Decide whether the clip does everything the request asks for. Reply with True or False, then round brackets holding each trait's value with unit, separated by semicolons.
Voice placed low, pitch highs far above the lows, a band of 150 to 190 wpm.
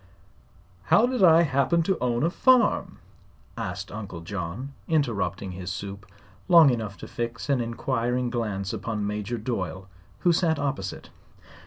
False (120 Hz; 6.4 semitones; 140 wpm)